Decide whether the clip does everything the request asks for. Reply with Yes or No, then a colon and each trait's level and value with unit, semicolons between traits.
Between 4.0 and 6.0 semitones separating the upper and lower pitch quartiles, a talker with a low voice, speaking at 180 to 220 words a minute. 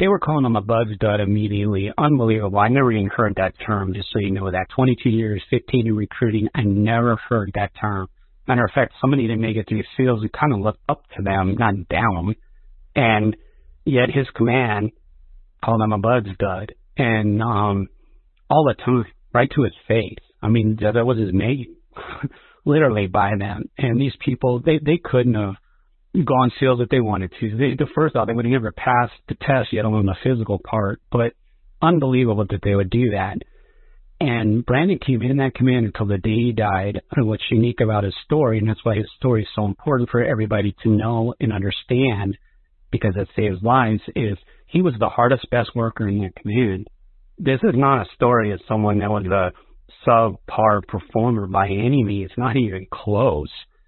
No: average, 3.6 semitones; low, 110 Hz; average, 195 wpm